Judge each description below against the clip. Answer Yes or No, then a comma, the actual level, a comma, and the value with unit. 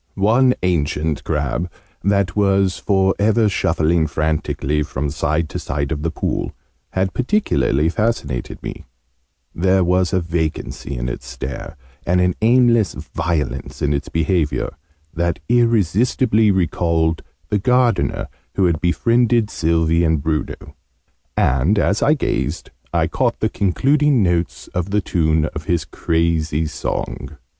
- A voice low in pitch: Yes, very low, 85 Hz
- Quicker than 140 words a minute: No, slow, 135 wpm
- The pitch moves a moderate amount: Yes, average, 4.7 semitones